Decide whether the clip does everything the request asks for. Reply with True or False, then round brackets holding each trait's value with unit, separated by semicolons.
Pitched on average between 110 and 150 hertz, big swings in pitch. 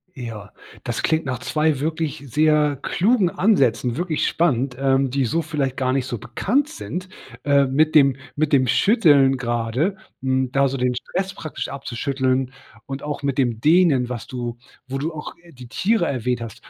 False (140 Hz; 3.7 semitones)